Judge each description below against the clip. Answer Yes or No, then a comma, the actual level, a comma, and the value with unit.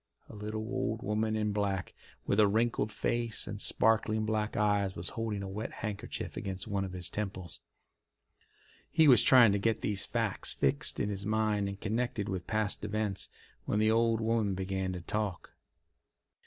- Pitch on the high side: No, low, 105 Hz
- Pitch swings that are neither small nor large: No, narrow, 2.0 semitones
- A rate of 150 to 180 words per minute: Yes, average, 170 wpm